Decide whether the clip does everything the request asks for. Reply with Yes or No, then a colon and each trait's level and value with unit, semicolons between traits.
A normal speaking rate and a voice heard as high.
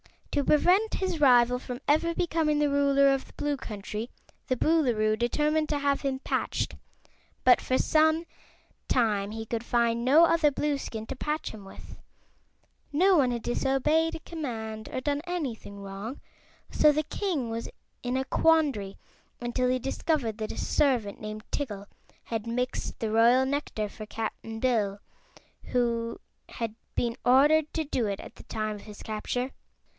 Yes: average, 160 wpm; very high, 255 Hz